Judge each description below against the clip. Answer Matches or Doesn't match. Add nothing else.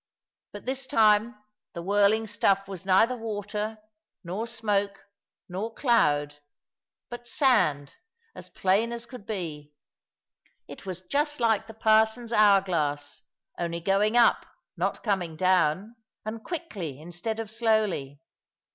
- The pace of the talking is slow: Matches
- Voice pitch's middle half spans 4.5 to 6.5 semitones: Doesn't match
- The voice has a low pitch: Doesn't match